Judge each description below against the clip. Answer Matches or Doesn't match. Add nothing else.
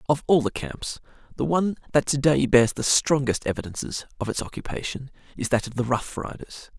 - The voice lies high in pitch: Doesn't match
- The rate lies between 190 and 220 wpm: Matches